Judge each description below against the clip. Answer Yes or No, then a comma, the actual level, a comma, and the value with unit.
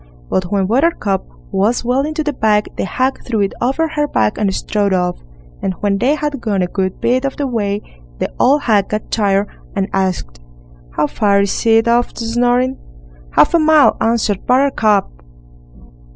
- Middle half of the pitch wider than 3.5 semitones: Yes, average, 4.7 semitones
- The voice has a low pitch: No, high, 220 Hz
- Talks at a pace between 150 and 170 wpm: No, average, 180 wpm